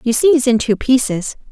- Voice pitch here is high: Yes, very high, 250 Hz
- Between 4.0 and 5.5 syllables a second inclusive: Yes, 5.4 syllables/s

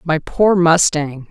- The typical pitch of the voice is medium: Yes, medium, 165 Hz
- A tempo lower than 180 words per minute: Yes, average, 140 wpm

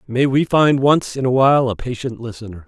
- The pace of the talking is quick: Yes, fast, 225 wpm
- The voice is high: No, low, 125 Hz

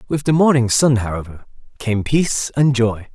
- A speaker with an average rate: Yes, average, 170 wpm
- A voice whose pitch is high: No, low, 125 Hz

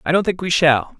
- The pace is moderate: No, fast, 300 wpm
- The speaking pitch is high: No, medium, 160 Hz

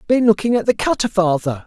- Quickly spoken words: Yes, fast, 215 wpm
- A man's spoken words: Yes, male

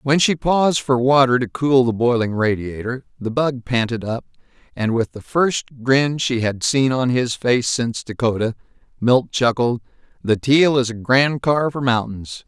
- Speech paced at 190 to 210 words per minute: No, average, 180 wpm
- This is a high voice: No, low, 125 Hz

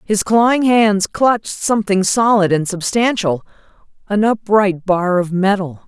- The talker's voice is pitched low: No, high, 200 Hz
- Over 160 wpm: No, slow, 135 wpm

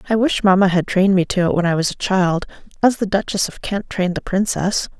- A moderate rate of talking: No, fast, 250 wpm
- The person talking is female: Yes, female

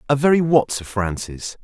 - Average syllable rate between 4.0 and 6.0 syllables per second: Yes, 4.9 syllables/s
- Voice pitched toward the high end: No, low, 125 Hz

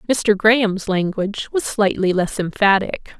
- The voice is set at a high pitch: Yes, high, 205 Hz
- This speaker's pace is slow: Yes, slow, 130 wpm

